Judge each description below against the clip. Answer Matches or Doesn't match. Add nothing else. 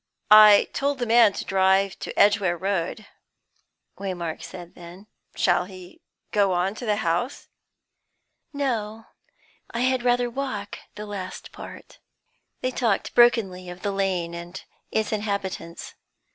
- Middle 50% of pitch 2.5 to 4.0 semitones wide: Matches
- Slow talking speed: Matches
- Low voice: Doesn't match